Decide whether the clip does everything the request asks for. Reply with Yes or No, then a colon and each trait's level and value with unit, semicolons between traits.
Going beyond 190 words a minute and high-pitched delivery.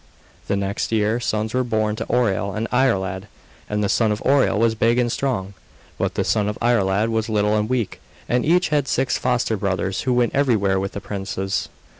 No: average, 200 wpm; low, 110 Hz